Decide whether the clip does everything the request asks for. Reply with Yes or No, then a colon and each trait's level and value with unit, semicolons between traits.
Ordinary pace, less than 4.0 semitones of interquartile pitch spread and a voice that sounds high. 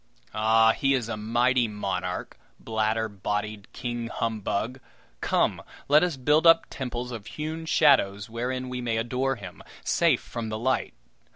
No: average, 150 wpm; average, 3.2 semitones; low, 115 Hz